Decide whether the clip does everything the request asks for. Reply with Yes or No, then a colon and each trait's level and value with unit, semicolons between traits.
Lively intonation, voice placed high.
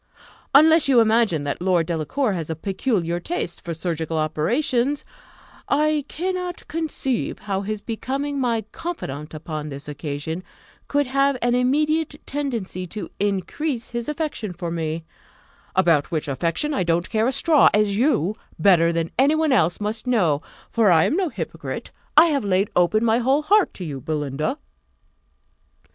Yes: wide, 8.9 semitones; high, 215 Hz